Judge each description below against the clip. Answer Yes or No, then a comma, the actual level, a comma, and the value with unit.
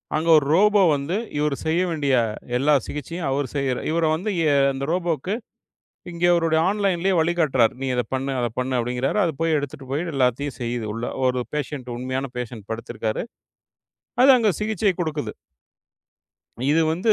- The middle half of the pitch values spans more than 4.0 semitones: Yes, average, 4.8 semitones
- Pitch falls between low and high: Yes, medium, 145 Hz